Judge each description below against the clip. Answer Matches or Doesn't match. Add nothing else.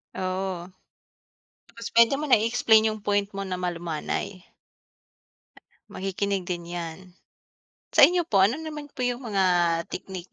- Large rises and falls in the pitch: Doesn't match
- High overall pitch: Matches